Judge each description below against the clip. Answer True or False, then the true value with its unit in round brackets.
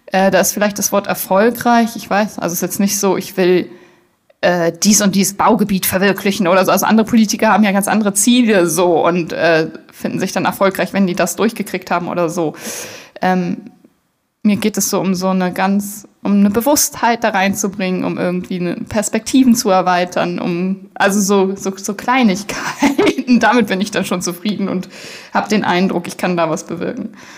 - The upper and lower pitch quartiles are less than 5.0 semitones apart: True (2.8 semitones)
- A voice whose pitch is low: False (195 Hz)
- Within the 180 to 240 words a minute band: True (190 wpm)